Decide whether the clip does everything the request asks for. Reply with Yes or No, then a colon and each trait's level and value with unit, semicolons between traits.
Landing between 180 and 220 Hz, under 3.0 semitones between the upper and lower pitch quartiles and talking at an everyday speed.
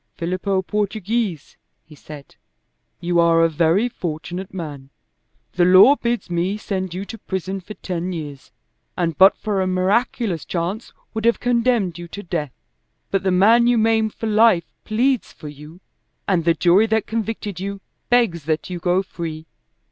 No: medium, 185 Hz; average, 4.4 semitones; average, 165 wpm